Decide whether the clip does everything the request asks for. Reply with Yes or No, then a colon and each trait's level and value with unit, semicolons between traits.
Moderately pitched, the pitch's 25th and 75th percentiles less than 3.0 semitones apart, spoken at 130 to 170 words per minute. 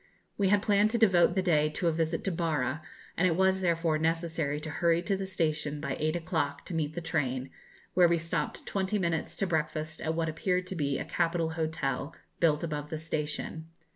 No: medium, 165 Hz; narrow, 2.4 semitones; fast, 205 wpm